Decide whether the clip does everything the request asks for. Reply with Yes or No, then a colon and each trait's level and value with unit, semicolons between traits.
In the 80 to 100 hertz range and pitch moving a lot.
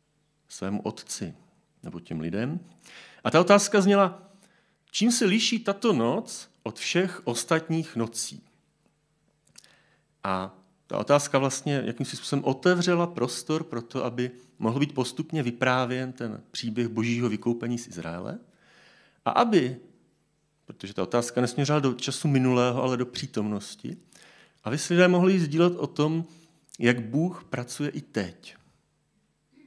No: low, 135 Hz; wide, 5.7 semitones